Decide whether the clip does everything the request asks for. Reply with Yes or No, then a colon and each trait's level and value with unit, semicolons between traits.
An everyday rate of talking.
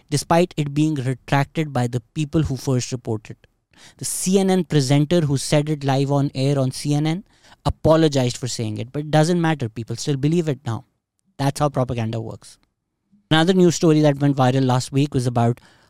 Yes: average, 180 wpm